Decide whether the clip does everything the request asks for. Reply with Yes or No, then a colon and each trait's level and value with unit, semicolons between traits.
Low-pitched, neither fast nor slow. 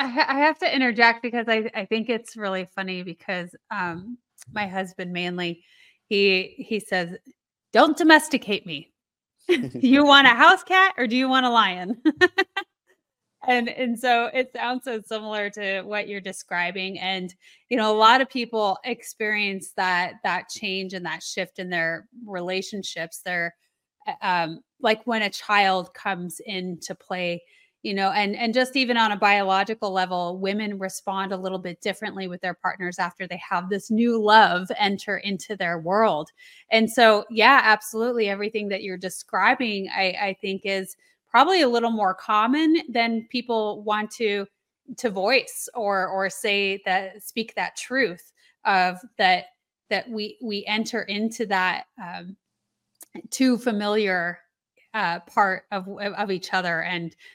No: high, 205 Hz; average, 155 wpm